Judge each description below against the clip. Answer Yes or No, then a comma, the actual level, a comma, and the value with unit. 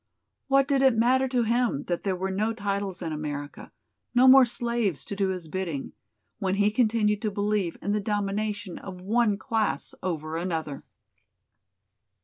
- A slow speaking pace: No, average, 160 wpm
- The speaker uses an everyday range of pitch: Yes, average, 4.0 semitones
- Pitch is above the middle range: Yes, high, 205 Hz